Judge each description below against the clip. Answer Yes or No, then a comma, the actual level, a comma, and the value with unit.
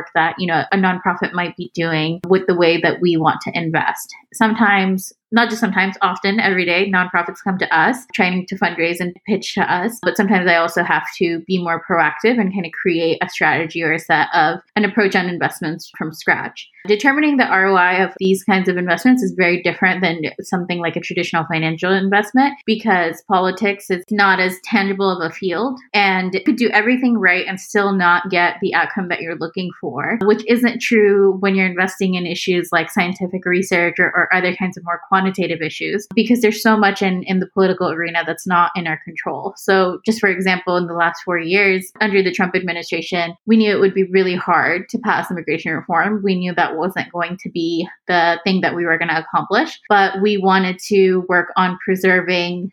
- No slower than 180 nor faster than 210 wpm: Yes, fast, 205 wpm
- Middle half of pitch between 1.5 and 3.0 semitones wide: Yes, narrow, 2.4 semitones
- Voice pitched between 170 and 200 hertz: Yes, medium, 185 Hz